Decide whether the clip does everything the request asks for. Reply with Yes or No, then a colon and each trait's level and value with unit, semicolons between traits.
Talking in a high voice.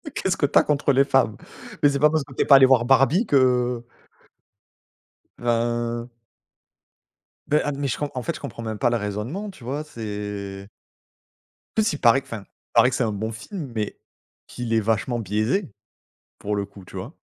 No: low, 120 Hz